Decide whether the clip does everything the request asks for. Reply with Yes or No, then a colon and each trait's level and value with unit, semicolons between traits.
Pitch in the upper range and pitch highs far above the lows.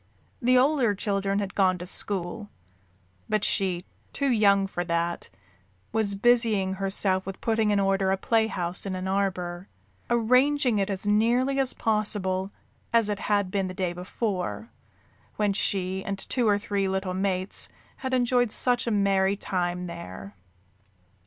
No: high, 200 Hz; average, 3.0 semitones